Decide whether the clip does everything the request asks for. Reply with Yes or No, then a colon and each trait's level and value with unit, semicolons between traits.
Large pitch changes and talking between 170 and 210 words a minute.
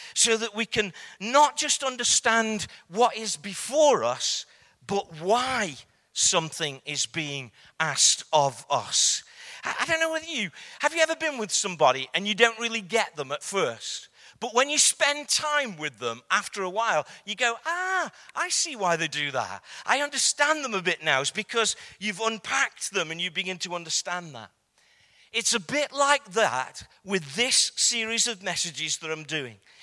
Yes: wide, 8.0 semitones; average, 175 wpm